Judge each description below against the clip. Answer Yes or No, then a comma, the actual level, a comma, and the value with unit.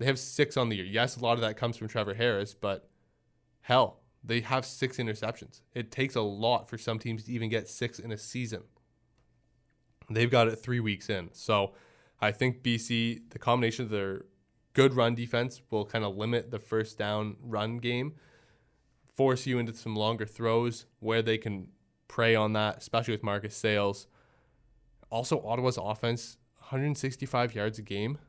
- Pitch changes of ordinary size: No, narrow, 2.2 semitones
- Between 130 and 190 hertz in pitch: No, low, 115 Hz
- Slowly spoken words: No, average, 180 wpm